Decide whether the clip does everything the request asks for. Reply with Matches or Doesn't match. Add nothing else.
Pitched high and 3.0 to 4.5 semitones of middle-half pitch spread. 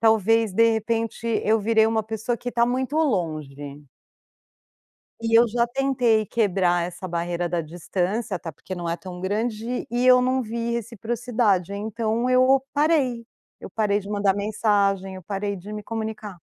Matches